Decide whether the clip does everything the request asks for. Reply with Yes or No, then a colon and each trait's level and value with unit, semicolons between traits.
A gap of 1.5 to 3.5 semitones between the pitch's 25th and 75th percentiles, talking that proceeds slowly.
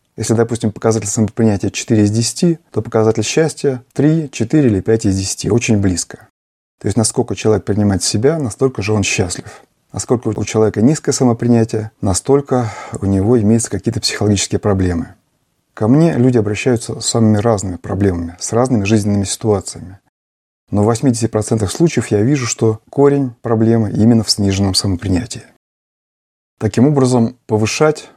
No: average, 3.1 semitones; average, 145 wpm